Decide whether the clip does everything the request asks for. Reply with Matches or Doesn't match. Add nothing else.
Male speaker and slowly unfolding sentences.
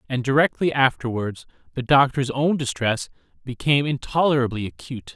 Matches